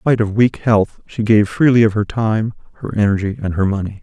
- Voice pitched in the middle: No, low, 105 Hz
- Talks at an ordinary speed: No, fast, 240 wpm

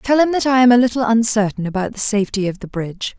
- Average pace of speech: No, fast, 265 wpm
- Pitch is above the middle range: Yes, high, 225 Hz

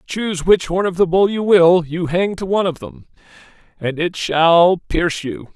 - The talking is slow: No, fast, 205 wpm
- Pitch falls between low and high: Yes, medium, 175 Hz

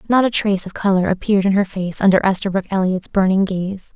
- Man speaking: No, female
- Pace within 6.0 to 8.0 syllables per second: Yes, 6.2 syllables/s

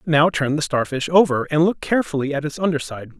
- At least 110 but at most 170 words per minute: No, fast, 205 wpm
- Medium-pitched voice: Yes, medium, 150 Hz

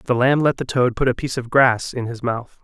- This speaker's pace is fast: Yes, fast, 295 wpm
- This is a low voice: Yes, low, 125 Hz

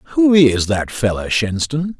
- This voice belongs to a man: Yes, male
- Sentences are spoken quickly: No, average, 150 wpm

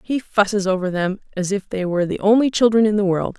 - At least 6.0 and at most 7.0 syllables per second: Yes, 6.1 syllables/s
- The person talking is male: No, female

